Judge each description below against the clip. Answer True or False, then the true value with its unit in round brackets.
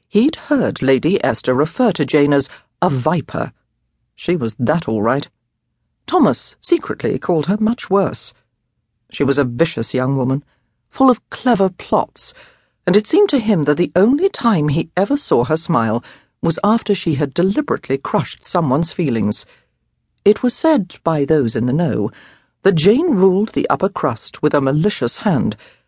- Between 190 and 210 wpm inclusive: False (165 wpm)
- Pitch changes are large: True (8.0 semitones)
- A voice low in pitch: False (165 Hz)